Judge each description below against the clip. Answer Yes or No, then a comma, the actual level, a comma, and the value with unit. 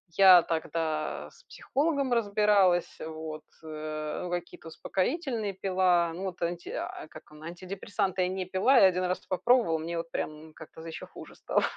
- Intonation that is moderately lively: Yes, average, 3.5 semitones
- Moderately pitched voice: Yes, medium, 180 Hz